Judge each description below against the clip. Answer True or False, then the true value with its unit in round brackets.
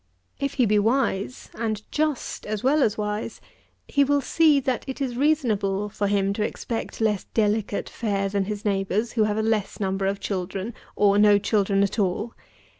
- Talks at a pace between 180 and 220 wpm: True (185 wpm)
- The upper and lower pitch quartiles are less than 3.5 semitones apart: True (3.1 semitones)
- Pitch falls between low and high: False (210 Hz)